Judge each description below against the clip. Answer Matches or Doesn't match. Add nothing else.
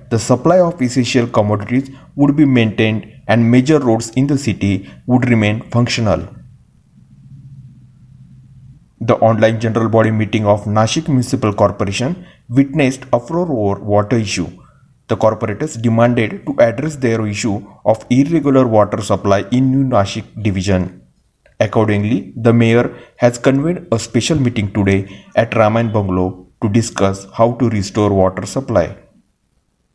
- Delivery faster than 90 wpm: Matches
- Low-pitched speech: Matches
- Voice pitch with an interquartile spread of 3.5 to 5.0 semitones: Matches